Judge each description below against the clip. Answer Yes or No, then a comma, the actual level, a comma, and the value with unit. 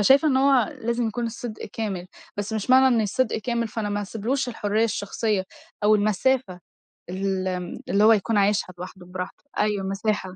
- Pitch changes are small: No, average, 3.1 semitones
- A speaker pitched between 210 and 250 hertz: Yes, high, 215 Hz